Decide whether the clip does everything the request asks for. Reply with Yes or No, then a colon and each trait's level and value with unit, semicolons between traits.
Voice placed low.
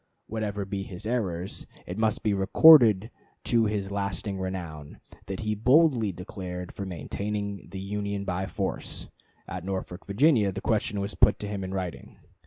Yes: low, 100 Hz